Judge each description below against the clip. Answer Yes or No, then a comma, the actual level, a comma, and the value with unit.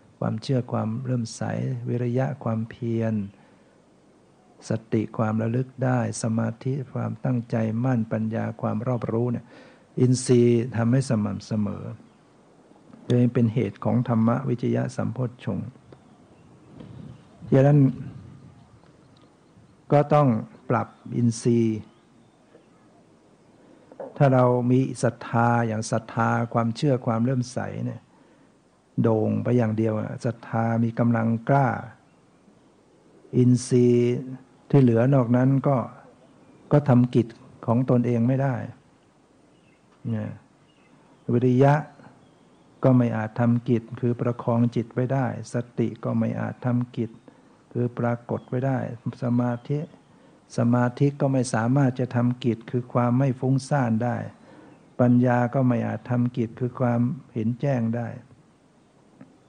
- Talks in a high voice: No, low, 120 Hz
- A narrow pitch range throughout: Yes, narrow, 1.9 semitones